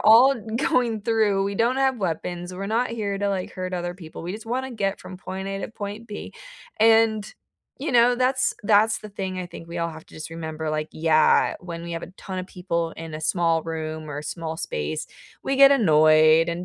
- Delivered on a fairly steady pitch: No, average, 5.1 semitones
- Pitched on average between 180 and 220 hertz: Yes, medium, 185 Hz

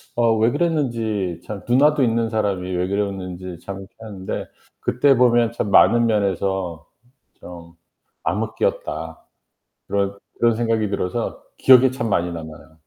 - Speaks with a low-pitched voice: Yes, low, 105 Hz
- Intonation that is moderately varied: Yes, average, 4.2 semitones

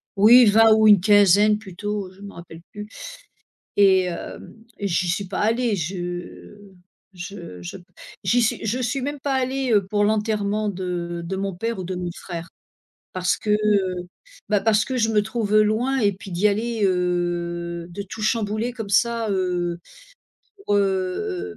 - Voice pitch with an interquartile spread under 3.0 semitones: No, average, 3.3 semitones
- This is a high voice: Yes, high, 205 Hz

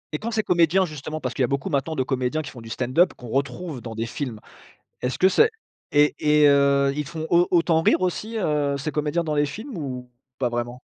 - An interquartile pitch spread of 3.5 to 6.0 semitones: Yes, average, 4.4 semitones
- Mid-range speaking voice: Yes, medium, 145 Hz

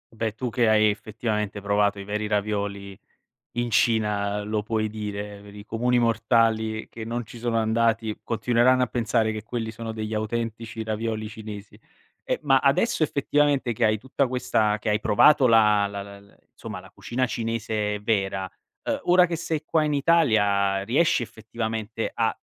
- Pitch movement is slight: Yes, narrow, 2.2 semitones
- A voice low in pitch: Yes, low, 110 Hz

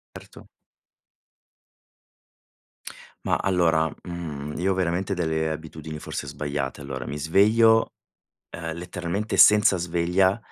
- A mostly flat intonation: No, average, 3.3 semitones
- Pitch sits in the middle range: No, very low, 85 Hz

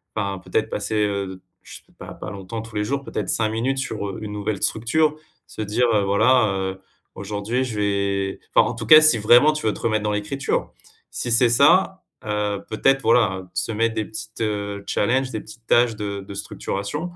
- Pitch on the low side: Yes, low, 110 Hz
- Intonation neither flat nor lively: Yes, average, 3.0 semitones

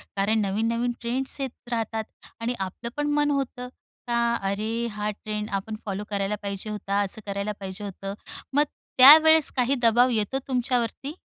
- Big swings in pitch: No, average, 3.6 semitones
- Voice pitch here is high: Yes, high, 225 Hz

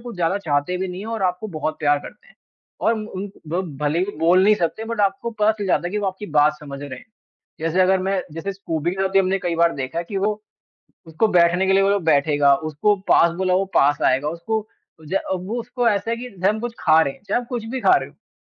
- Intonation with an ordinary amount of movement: Yes, average, 4.3 semitones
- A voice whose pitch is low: No, high, 190 Hz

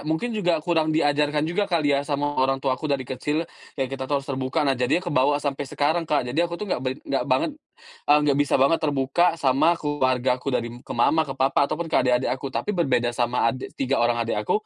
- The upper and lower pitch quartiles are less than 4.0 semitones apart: Yes, average, 3.3 semitones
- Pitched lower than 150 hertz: Yes, medium, 140 Hz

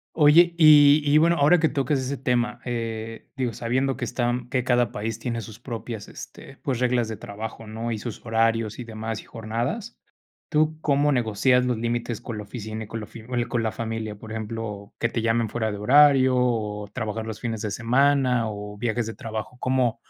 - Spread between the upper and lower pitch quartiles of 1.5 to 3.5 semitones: Yes, average, 2.8 semitones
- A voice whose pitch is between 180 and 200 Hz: No, low, 115 Hz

